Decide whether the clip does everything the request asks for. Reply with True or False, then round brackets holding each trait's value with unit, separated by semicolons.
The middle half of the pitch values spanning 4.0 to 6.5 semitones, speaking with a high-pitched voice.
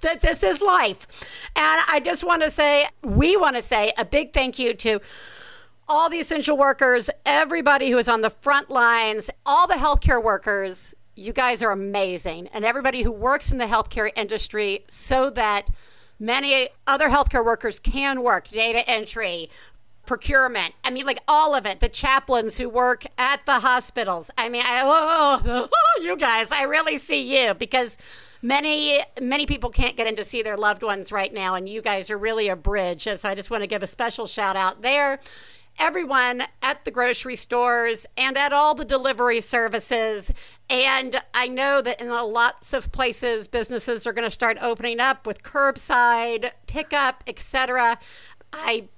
False (3.6 semitones; 245 Hz)